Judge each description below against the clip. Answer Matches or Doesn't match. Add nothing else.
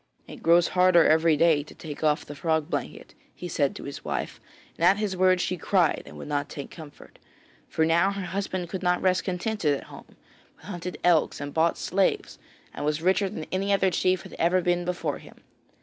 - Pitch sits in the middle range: Matches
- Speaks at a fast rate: Matches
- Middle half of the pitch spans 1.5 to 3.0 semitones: Matches